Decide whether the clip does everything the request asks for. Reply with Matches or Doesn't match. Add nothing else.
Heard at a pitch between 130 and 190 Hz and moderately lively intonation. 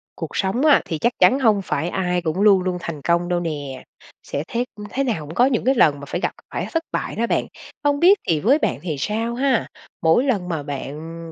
Doesn't match